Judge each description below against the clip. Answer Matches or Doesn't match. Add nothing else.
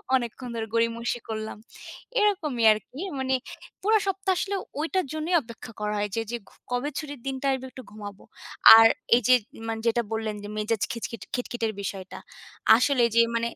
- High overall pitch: Matches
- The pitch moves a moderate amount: Matches